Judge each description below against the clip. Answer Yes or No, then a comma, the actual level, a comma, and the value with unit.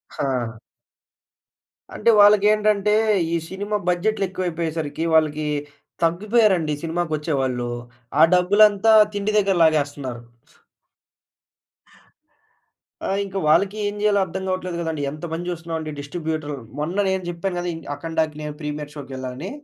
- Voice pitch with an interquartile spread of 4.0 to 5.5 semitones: Yes, average, 4.5 semitones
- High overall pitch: No, medium, 170 Hz